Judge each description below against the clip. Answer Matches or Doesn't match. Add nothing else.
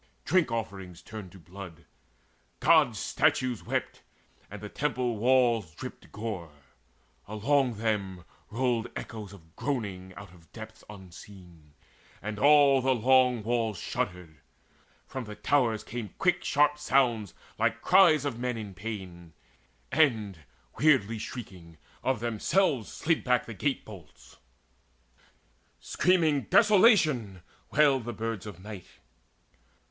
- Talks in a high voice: Doesn't match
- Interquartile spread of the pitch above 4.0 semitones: Matches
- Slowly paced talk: Matches